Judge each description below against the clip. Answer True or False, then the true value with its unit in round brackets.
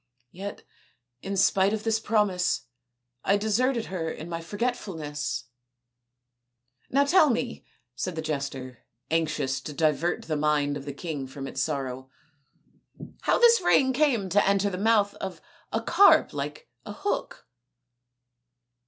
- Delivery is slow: False (145 wpm)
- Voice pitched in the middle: True (180 Hz)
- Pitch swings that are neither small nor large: False (7.2 semitones)